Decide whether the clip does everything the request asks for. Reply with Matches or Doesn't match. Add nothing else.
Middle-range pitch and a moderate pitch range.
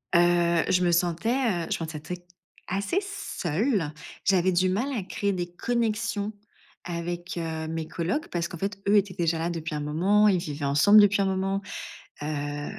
Matches